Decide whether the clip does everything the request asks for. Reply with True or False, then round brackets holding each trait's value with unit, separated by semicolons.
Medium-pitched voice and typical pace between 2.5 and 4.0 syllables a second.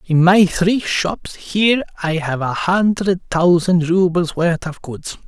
True (175 Hz; 3.7 syllables/s)